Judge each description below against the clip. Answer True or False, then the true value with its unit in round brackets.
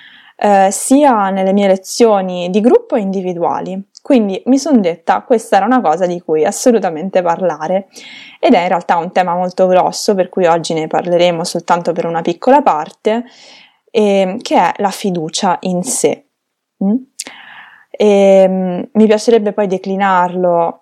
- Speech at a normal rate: True (155 wpm)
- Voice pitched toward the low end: False (195 Hz)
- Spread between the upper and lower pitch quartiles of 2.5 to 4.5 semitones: False (5.1 semitones)